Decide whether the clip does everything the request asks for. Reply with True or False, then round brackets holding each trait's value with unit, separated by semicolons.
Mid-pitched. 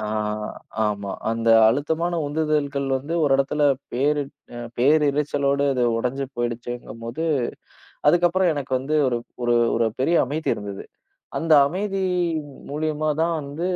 True (145 Hz)